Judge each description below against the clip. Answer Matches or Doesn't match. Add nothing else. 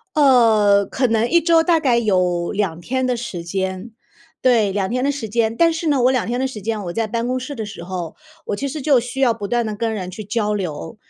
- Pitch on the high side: Matches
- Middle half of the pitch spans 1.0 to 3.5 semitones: Doesn't match